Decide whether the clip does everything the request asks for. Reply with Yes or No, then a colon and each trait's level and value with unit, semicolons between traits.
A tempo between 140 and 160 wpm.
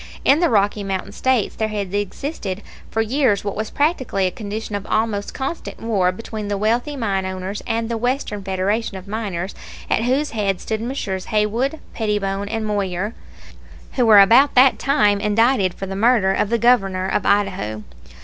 No: average, 175 wpm